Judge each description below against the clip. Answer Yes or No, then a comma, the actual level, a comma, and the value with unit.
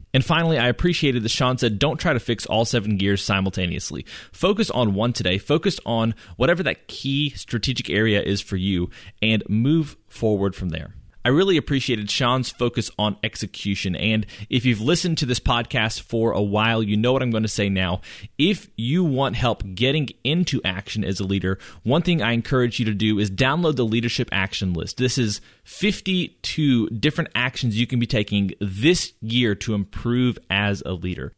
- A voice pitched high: No, low, 115 Hz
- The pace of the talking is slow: No, average, 185 wpm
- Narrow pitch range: No, average, 4.3 semitones